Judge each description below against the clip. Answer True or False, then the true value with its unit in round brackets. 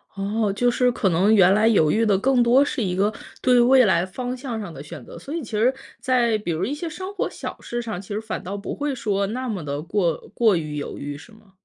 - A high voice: True (215 Hz)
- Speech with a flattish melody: False (4.7 semitones)